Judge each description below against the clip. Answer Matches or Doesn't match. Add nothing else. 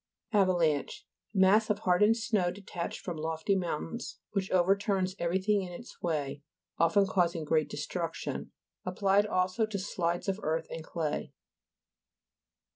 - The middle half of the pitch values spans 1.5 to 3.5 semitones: Matches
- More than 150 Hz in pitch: Matches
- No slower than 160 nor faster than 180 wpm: Doesn't match